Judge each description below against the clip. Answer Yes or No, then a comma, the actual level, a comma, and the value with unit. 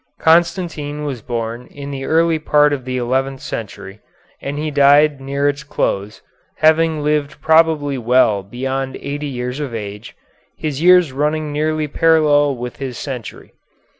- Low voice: No, medium, 145 Hz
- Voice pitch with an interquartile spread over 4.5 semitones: No, average, 3.1 semitones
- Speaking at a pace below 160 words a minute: Yes, average, 140 wpm